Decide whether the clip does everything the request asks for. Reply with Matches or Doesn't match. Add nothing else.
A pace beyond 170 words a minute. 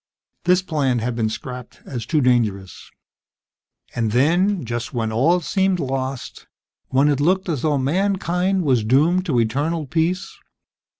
Doesn't match